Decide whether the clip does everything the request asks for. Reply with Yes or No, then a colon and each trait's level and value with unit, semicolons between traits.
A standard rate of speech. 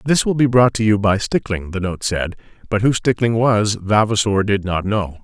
No: fast, 220 wpm